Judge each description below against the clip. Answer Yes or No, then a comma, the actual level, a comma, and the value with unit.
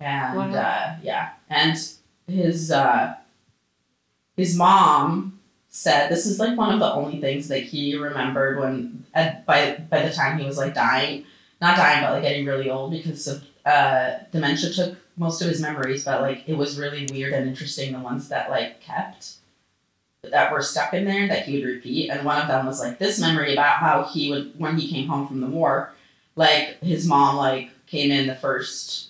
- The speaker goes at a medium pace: Yes, average, 195 wpm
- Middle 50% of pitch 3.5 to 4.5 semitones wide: No, average, 3.1 semitones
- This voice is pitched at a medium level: Yes, medium, 145 Hz